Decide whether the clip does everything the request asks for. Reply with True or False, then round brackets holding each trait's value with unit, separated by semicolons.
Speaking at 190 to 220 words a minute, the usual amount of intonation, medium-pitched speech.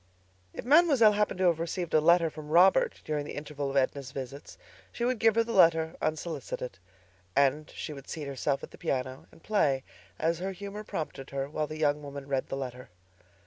True (200 wpm; 5.0 semitones; 155 Hz)